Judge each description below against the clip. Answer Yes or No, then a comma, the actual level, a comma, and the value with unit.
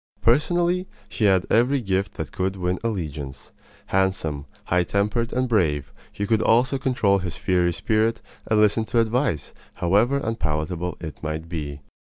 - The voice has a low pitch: Yes, low, 100 Hz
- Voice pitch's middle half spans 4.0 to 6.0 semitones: Yes, average, 5.1 semitones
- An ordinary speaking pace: Yes, average, 150 wpm